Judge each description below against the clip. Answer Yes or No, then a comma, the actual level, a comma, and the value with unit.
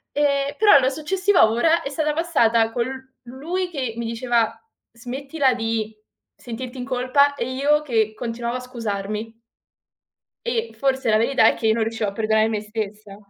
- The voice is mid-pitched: No, high, 245 Hz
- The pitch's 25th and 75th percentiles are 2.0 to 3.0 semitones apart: No, average, 3.9 semitones